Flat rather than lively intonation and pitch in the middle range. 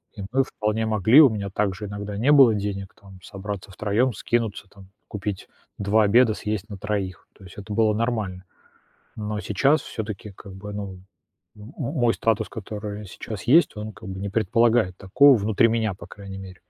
No: narrow, 2.2 semitones; low, 105 Hz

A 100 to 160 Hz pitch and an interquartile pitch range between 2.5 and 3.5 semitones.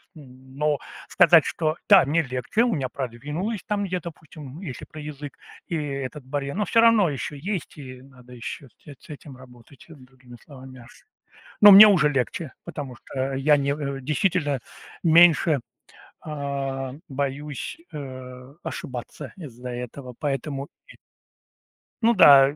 Yes: medium, 140 Hz; average, 3.2 semitones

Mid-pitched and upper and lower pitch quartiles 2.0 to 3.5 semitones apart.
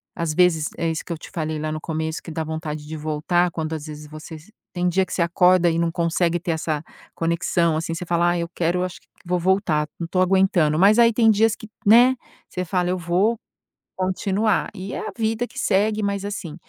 Yes: medium, 175 Hz; average, 3.1 semitones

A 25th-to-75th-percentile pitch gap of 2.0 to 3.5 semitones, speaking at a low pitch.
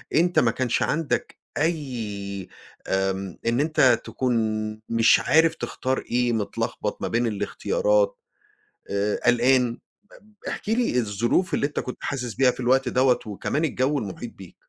No: average, 4.8 semitones; low, 125 Hz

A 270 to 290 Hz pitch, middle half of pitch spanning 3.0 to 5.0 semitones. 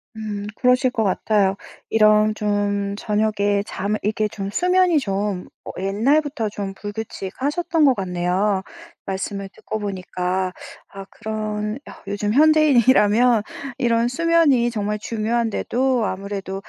No: high, 210 Hz; average, 3.3 semitones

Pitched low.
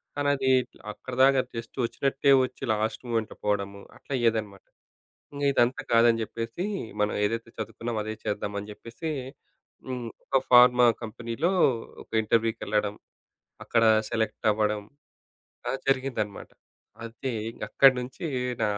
Yes: low, 115 Hz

